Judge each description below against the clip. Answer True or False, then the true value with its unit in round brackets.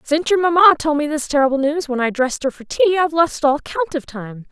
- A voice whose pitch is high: True (295 Hz)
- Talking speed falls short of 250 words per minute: False (265 wpm)